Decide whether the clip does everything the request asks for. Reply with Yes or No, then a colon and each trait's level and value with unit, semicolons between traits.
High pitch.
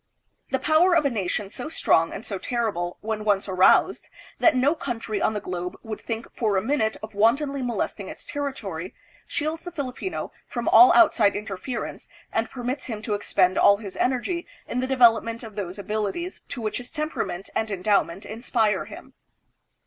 Yes: high, 225 Hz